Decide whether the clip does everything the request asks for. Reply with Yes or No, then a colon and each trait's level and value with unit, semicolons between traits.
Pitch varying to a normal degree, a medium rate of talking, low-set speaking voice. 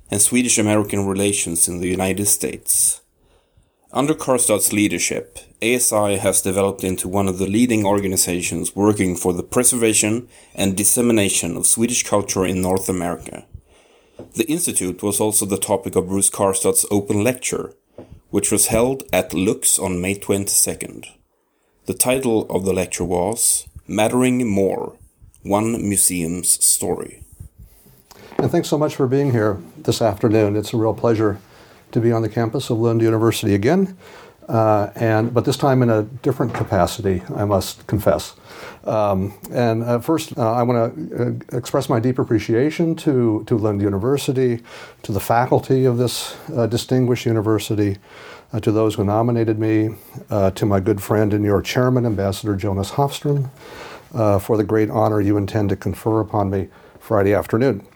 Yes: average, 3.4 semitones; average, 155 wpm; low, 110 Hz